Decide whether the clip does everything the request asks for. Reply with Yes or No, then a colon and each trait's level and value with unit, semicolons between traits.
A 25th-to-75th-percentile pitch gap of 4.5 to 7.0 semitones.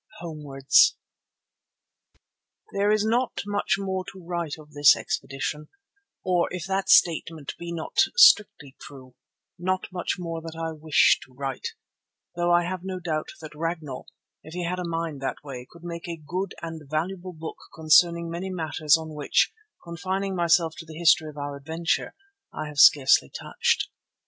No: average, 2.9 semitones